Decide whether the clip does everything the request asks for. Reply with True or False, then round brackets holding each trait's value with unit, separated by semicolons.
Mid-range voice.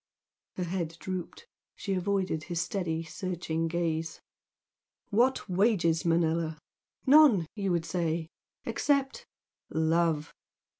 True (170 Hz)